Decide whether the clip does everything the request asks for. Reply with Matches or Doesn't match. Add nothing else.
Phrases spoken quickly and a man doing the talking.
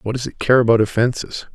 Matches